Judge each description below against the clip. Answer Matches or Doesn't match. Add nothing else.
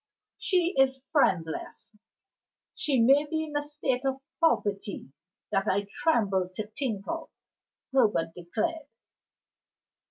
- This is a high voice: Matches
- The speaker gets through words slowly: Matches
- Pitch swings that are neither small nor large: Doesn't match